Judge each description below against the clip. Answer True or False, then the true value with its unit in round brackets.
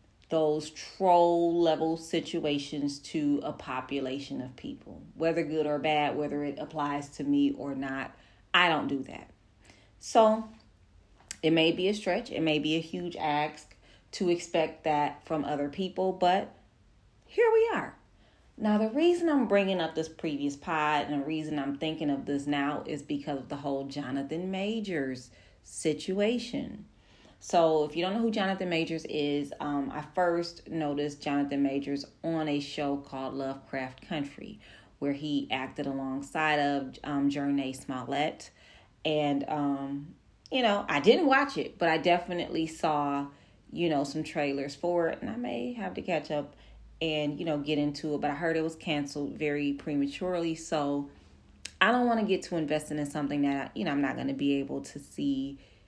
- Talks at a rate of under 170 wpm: False (175 wpm)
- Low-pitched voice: False (150 Hz)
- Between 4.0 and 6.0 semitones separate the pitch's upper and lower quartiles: False (3.0 semitones)